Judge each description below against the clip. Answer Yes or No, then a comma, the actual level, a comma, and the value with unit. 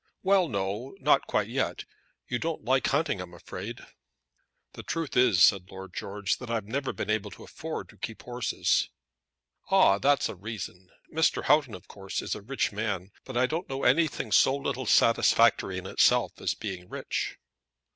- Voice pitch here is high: No, low, 115 Hz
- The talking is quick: No, average, 175 wpm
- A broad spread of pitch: Yes, wide, 5.7 semitones